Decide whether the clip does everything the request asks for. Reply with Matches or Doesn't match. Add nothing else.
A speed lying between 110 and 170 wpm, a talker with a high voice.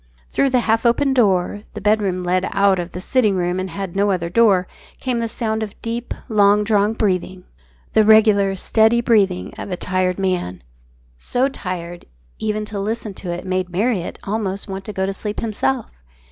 Doesn't match